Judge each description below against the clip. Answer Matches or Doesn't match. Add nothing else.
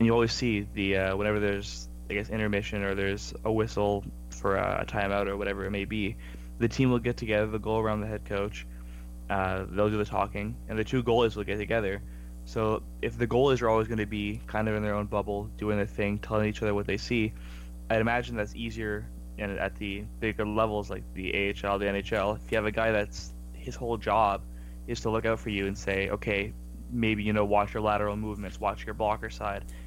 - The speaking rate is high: Matches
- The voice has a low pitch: Matches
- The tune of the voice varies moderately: Doesn't match